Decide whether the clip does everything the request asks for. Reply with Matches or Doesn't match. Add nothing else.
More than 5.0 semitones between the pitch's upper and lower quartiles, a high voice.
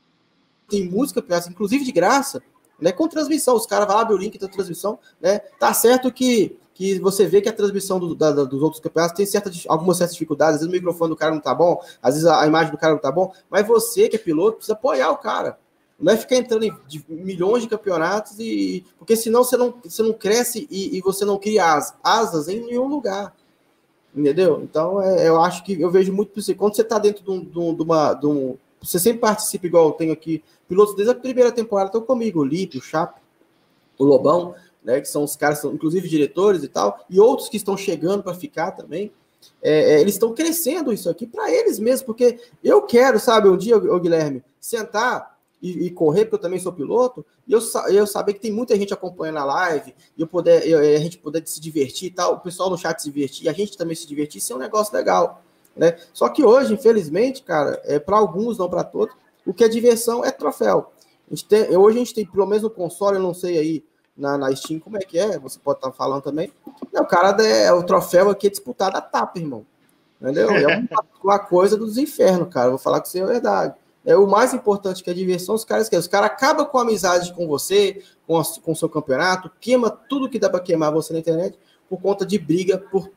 Matches